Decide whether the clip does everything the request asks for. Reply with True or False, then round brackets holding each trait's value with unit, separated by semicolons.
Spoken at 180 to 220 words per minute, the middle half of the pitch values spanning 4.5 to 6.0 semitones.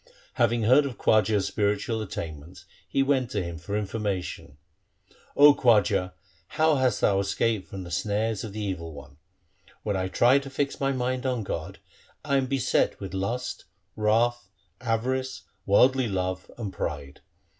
False (155 wpm; 5.2 semitones)